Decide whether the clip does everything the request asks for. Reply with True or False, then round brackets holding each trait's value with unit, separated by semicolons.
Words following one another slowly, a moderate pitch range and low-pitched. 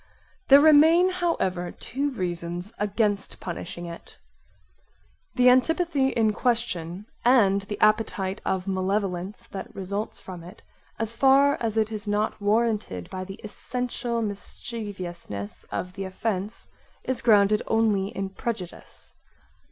False (120 wpm; 3.9 semitones; 210 Hz)